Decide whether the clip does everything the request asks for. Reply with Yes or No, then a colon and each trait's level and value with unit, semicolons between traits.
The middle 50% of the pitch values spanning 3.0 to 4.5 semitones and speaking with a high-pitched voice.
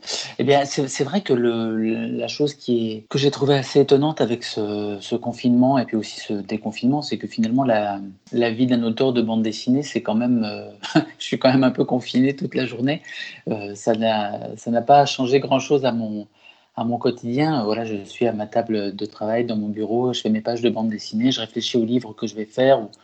No: average, 3.4 semitones; low, 120 Hz